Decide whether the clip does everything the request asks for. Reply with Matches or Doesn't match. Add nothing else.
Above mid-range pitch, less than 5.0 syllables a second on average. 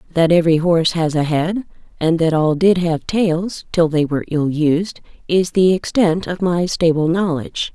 Doesn't match